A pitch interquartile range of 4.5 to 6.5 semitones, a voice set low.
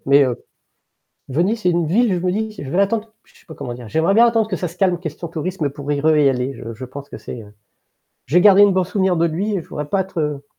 No: average, 5.3 semitones; medium, 170 Hz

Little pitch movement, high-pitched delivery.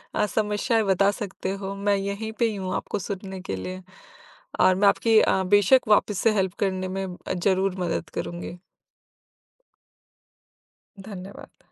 Yes: narrow, 1.8 semitones; high, 195 Hz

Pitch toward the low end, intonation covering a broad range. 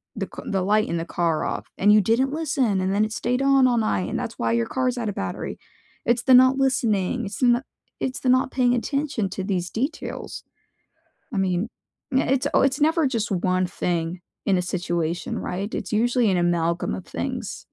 No: high, 215 Hz; wide, 5.8 semitones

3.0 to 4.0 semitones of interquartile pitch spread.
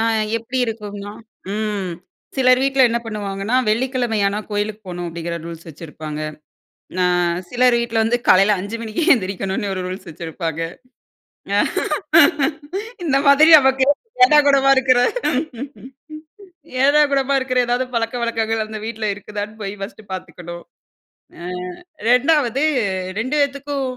No: average, 4.7 semitones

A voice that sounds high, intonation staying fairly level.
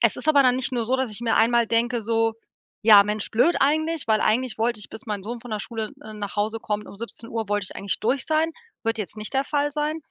No: high, 230 Hz; average, 3.3 semitones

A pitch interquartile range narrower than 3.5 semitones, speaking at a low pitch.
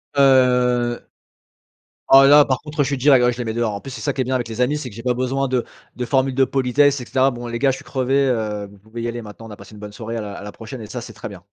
Yes: average, 2.8 semitones; low, 125 Hz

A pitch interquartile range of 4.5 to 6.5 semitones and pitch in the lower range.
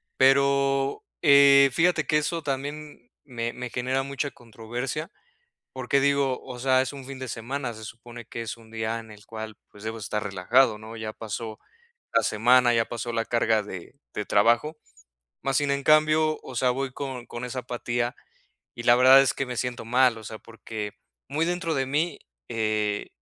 No: average, 3.4 semitones; low, 125 Hz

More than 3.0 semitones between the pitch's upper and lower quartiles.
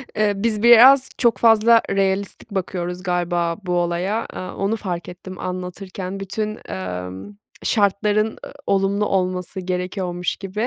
No: average, 2.7 semitones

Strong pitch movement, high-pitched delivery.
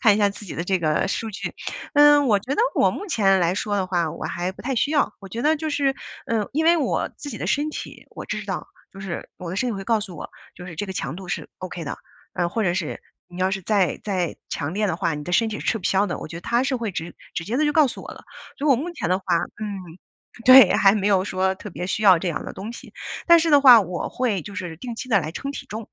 Yes: wide, 5.7 semitones; high, 200 Hz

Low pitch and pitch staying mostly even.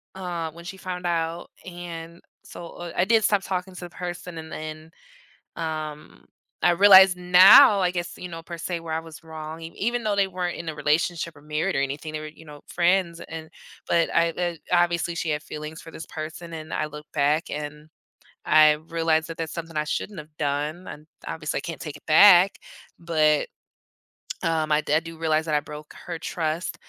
No: medium, 165 Hz; narrow, 2.2 semitones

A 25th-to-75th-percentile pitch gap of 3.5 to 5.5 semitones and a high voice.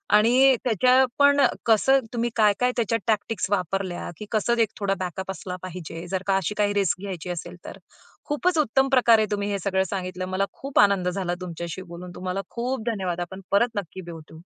Yes: average, 4.2 semitones; high, 200 Hz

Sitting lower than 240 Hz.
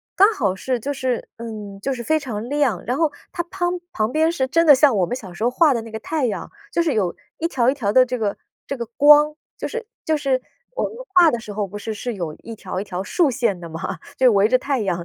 No: very high, 250 Hz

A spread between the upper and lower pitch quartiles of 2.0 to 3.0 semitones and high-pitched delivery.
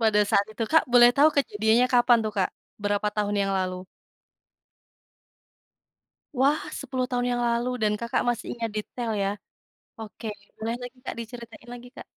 Yes: narrow, 2.5 semitones; high, 235 Hz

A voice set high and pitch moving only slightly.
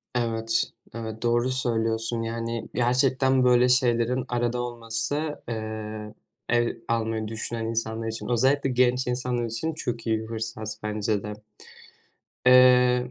No: low, 115 Hz; narrow, 1.9 semitones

